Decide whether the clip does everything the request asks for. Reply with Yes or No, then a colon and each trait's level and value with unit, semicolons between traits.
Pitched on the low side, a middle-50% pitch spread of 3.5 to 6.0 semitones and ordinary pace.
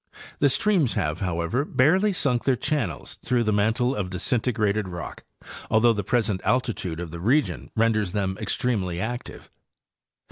Yes: low, 110 Hz; average, 5.3 semitones; average, 145 wpm